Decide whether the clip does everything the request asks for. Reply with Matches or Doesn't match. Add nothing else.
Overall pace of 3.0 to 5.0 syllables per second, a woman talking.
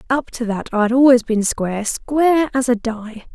Matches